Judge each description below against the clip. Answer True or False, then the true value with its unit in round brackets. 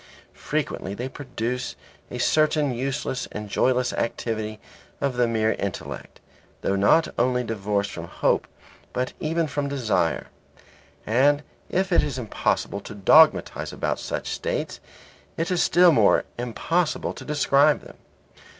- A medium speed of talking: False (130 wpm)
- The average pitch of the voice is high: False (125 Hz)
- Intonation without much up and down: False (5.4 semitones)